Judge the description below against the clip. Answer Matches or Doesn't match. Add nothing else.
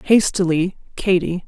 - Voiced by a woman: Matches